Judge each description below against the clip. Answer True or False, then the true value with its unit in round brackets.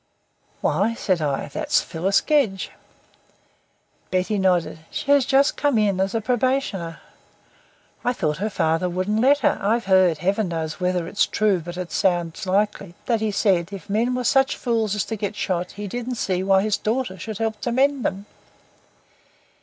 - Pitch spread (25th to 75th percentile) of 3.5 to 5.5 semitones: True (4.2 semitones)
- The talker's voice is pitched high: True (200 Hz)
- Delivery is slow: False (175 wpm)